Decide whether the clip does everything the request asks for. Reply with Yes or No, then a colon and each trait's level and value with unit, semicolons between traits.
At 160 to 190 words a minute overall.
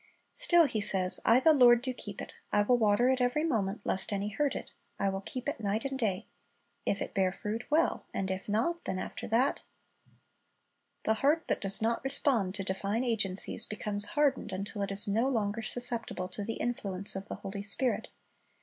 No: average, 200 wpm